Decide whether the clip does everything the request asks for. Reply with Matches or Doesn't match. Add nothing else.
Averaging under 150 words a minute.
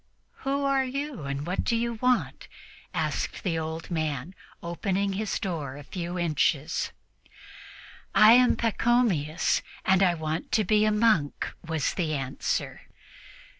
Matches